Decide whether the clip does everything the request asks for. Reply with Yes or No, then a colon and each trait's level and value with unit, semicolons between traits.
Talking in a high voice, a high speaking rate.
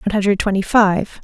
No: high, 200 Hz; average, 195 wpm